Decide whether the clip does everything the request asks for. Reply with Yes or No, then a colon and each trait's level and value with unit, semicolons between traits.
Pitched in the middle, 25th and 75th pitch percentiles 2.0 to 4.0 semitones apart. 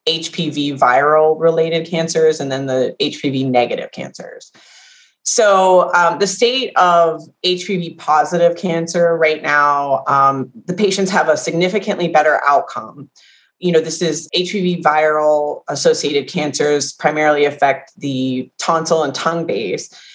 Yes: medium, 165 Hz; average, 3.4 semitones